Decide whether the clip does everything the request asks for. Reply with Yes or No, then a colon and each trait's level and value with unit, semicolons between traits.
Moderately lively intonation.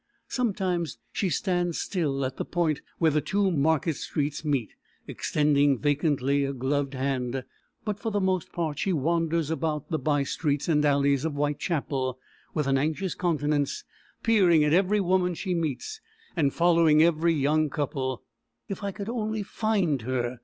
Yes: average, 3.9 semitones